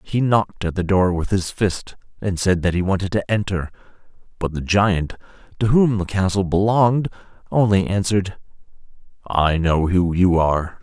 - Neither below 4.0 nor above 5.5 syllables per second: Yes, 5.0 syllables/s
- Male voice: Yes, male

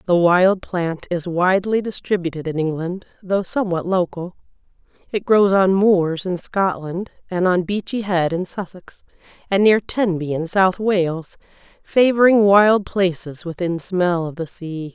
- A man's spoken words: No, female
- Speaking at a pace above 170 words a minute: No, average, 150 wpm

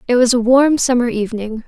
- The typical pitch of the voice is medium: No, high, 240 Hz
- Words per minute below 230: Yes, fast, 215 wpm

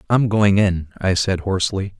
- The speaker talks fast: No, average, 180 wpm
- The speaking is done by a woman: No, male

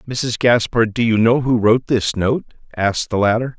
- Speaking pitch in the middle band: No, low, 115 Hz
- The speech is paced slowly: No, average, 200 wpm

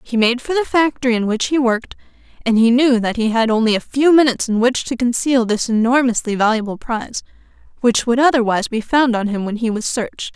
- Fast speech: Yes, fast, 220 wpm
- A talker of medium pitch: No, high, 240 Hz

